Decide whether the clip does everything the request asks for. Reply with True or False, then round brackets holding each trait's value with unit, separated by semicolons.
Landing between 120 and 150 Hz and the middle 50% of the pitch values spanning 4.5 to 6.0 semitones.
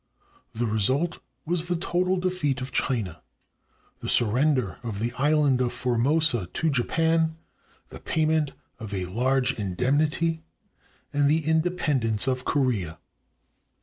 True (135 Hz; 5.2 semitones)